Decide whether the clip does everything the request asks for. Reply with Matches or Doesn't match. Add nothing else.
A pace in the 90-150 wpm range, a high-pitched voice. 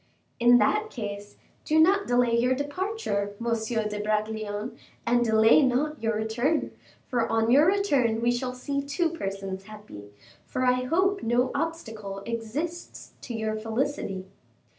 Matches